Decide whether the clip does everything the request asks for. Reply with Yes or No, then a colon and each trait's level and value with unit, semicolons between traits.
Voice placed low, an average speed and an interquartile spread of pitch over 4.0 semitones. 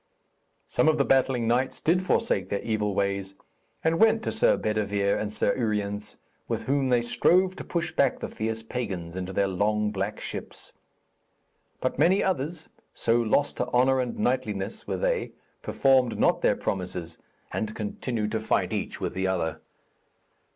Yes: low, 110 Hz; average, 165 wpm; average, 5.0 semitones